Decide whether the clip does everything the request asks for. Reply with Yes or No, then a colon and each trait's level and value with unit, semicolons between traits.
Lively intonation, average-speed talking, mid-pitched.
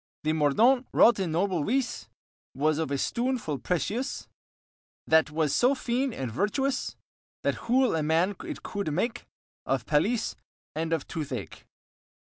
Yes: wide, 7.7 semitones; average, 150 wpm; medium, 180 Hz